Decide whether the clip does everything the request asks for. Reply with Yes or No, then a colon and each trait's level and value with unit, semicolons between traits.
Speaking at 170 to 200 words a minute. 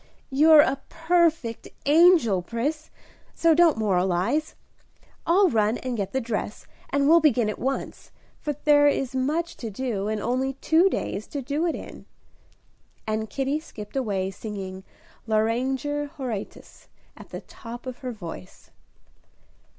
No: average, 140 wpm